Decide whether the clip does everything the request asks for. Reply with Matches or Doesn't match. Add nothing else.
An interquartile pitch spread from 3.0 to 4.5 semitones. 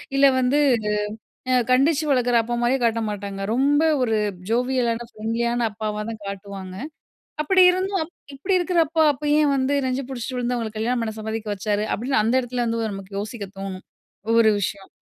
Matches